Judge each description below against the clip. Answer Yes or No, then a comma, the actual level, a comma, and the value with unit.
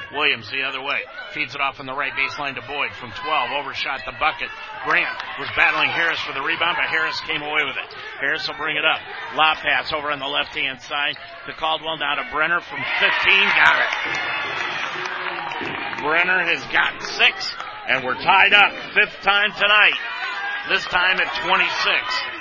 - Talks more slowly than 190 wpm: Yes, average, 180 wpm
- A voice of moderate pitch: Yes, medium, 155 Hz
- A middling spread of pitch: No, wide, 5.9 semitones